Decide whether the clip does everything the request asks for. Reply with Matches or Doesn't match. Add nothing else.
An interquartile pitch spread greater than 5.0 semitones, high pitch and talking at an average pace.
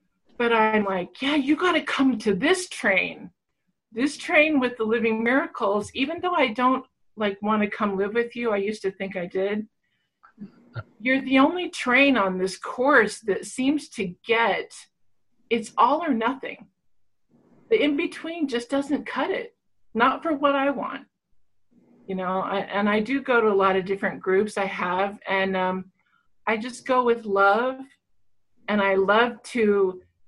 Matches